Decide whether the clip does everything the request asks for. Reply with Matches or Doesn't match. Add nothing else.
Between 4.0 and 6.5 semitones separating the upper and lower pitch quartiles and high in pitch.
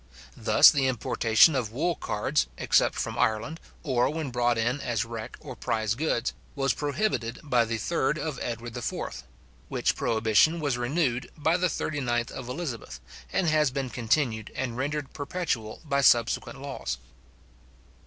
Doesn't match